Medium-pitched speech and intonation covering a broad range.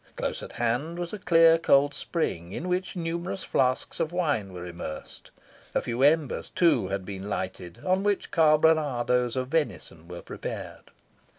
Yes: medium, 145 Hz; wide, 8.6 semitones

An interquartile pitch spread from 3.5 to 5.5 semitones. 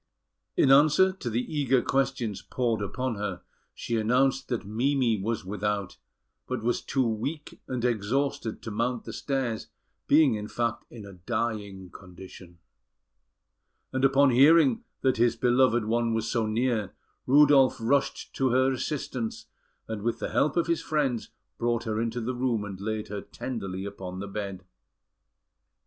Yes: average, 3.8 semitones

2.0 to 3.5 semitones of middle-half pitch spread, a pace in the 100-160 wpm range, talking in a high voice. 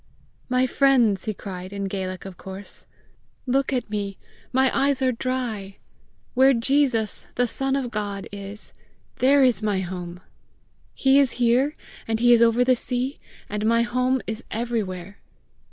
No: average, 4.3 semitones; average, 155 wpm; high, 235 Hz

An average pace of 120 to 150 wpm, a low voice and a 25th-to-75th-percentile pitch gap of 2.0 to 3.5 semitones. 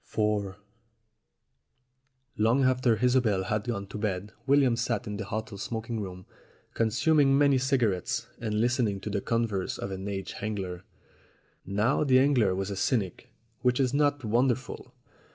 No: average, 145 wpm; low, 110 Hz; average, 4.2 semitones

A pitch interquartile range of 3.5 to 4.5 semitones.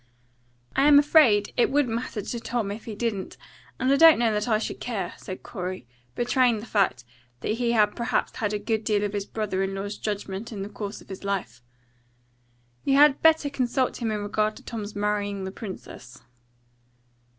No: average, 3.1 semitones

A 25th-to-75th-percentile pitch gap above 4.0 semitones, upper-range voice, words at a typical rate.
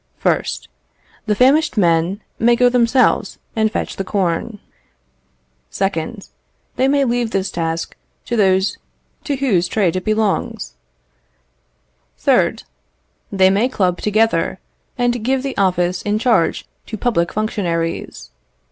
No: average, 4.6 semitones; high, 210 Hz; slow, 120 wpm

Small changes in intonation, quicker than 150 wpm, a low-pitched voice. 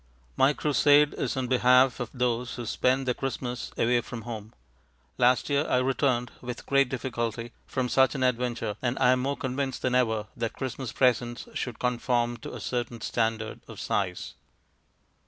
Yes: narrow, 1.7 semitones; average, 170 wpm; low, 125 Hz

